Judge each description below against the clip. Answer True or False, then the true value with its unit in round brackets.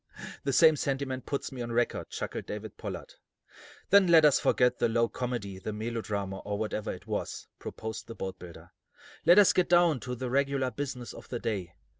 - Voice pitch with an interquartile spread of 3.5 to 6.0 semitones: True (4.4 semitones)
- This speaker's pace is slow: False (185 wpm)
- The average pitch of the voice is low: True (120 Hz)